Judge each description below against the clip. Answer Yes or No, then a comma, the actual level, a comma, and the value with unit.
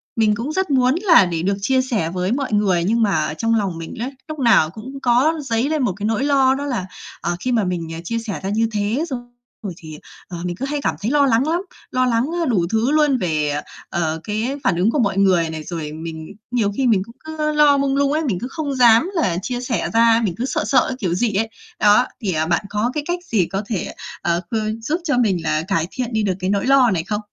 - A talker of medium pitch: No, high, 225 Hz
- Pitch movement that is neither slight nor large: No, wide, 6.1 semitones